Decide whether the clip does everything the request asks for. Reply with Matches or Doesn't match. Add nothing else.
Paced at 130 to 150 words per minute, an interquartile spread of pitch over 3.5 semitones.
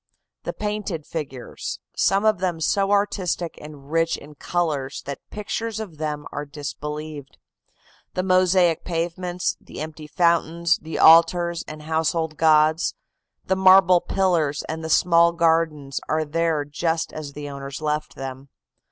Doesn't match